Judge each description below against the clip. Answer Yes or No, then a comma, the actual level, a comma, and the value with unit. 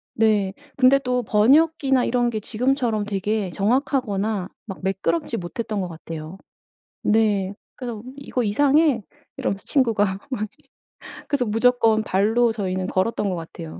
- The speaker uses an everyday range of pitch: Yes, average, 4.2 semitones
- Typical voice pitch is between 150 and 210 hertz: No, high, 220 Hz